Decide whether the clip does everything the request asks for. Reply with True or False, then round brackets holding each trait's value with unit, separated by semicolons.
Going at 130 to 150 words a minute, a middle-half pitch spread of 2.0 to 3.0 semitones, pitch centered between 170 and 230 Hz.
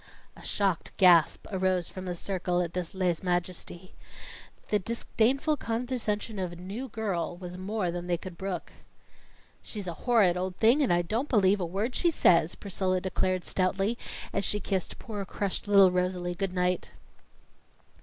False (160 wpm; 2.7 semitones; 185 Hz)